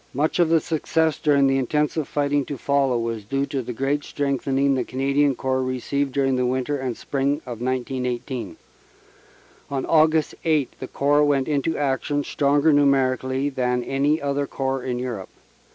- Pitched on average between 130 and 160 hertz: Yes, low, 135 Hz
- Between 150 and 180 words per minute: Yes, average, 165 wpm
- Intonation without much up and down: Yes, narrow, 2.0 semitones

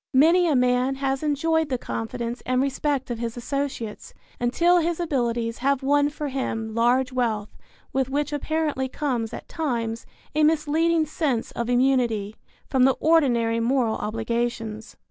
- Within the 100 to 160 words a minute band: Yes, average, 145 wpm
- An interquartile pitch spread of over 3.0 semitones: Yes, average, 3.9 semitones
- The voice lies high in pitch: Yes, very high, 260 Hz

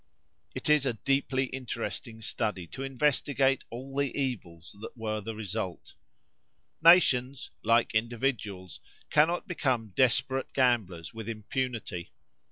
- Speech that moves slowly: Yes, slow, 115 wpm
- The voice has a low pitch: Yes, low, 120 Hz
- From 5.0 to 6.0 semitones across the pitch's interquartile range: No, average, 3.8 semitones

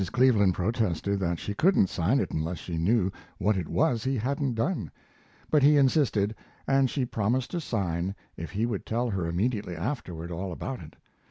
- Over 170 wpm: Yes, average, 180 wpm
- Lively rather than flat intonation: Yes, wide, 6.5 semitones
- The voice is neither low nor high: No, low, 105 Hz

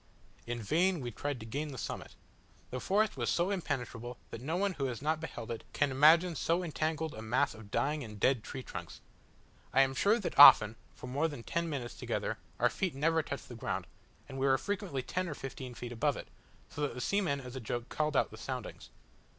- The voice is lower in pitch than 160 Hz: Yes, medium, 140 Hz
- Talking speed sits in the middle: No, fast, 215 wpm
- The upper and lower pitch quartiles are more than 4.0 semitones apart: Yes, average, 4.9 semitones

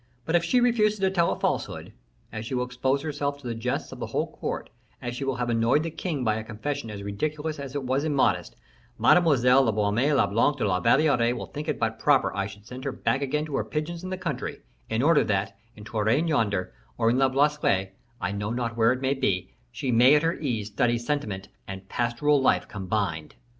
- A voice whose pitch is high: No, low, 125 Hz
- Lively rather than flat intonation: No, average, 5.0 semitones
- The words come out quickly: Yes, fast, 225 wpm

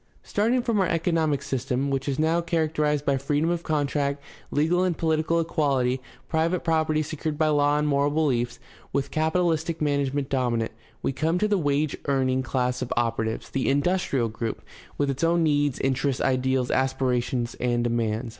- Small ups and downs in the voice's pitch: No, average, 3.4 semitones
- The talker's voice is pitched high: No, medium, 145 Hz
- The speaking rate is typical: Yes, average, 165 wpm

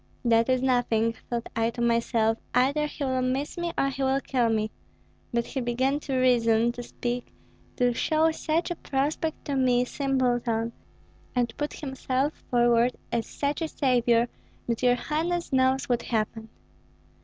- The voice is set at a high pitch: Yes, very high, 250 Hz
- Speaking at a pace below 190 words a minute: Yes, average, 160 wpm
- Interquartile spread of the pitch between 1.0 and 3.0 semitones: Yes, narrow, 2.6 semitones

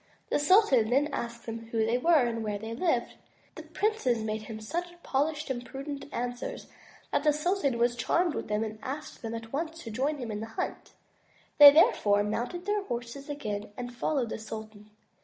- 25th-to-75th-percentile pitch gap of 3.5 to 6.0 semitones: Yes, average, 5.1 semitones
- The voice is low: No, high, 245 Hz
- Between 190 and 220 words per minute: Yes, average, 195 wpm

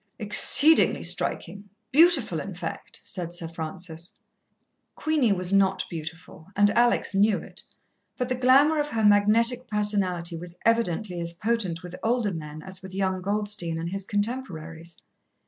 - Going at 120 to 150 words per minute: Yes, average, 145 wpm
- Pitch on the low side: No, high, 195 Hz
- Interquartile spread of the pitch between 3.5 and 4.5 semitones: No, average, 5.0 semitones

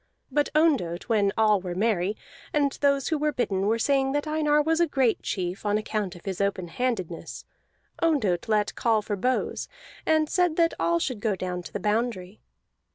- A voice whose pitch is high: Yes, high, 225 Hz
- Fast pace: No, average, 185 wpm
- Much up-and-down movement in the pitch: Yes, wide, 7.0 semitones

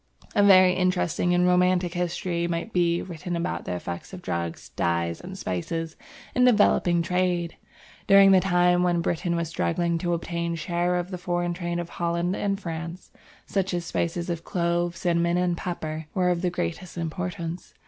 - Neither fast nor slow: Yes, average, 170 wpm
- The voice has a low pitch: No, medium, 175 Hz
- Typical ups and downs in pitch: No, narrow, 1.2 semitones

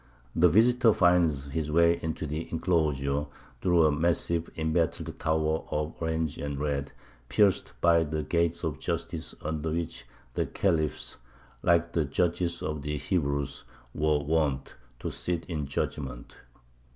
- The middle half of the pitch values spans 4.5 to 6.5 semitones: No, narrow, 2.4 semitones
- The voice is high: No, very low, 80 Hz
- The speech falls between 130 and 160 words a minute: Yes, average, 140 wpm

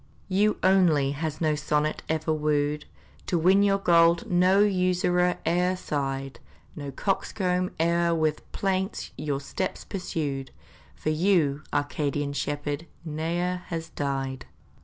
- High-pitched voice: No, medium, 160 Hz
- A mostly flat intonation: No, average, 3.8 semitones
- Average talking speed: No, slow, 120 wpm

